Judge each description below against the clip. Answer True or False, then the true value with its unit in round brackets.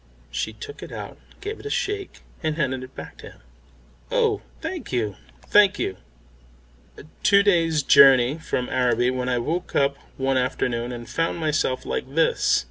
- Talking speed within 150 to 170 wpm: True (165 wpm)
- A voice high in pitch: False (140 Hz)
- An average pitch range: False (5.9 semitones)